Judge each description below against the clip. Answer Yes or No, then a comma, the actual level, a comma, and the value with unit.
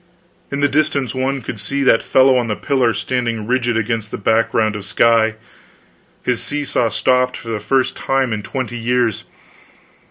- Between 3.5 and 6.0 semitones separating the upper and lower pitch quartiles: No, average, 2.8 semitones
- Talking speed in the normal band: Yes, average, 165 wpm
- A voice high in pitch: No, low, 120 Hz